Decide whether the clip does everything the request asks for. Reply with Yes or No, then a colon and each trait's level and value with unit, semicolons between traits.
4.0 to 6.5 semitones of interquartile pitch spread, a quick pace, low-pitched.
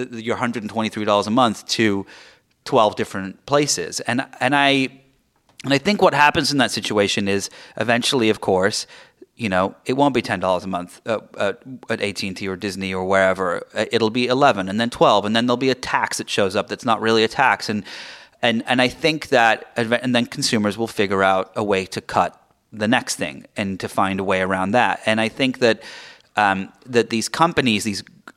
Yes: average, 4.4 semitones; fast, 210 wpm; low, 115 Hz